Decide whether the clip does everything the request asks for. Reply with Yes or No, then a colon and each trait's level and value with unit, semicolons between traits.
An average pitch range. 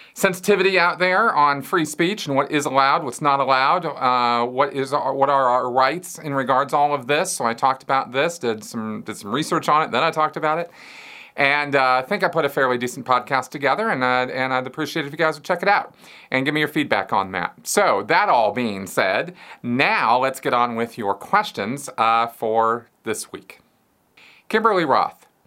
Yes: average, 3.7 semitones